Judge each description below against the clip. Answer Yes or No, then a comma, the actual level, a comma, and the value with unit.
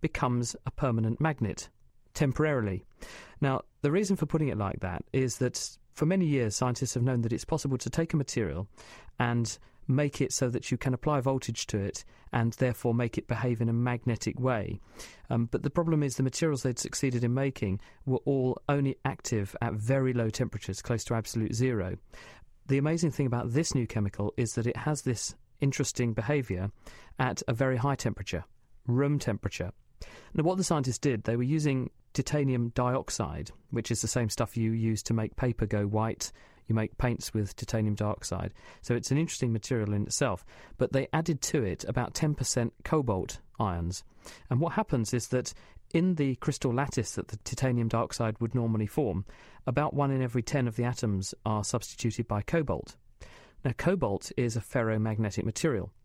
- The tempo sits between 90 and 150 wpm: No, average, 180 wpm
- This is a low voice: Yes, low, 120 Hz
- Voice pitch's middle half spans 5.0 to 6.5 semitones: No, average, 3.6 semitones